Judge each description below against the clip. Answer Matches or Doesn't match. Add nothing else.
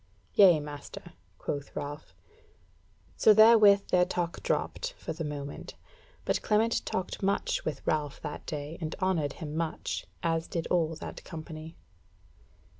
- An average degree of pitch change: Matches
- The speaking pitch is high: Doesn't match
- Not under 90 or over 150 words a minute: Matches